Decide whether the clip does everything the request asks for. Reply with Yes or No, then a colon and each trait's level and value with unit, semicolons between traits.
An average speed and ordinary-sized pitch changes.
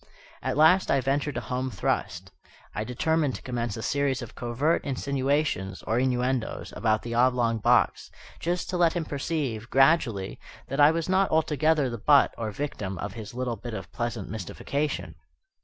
Yes: average, 170 wpm; average, 4.4 semitones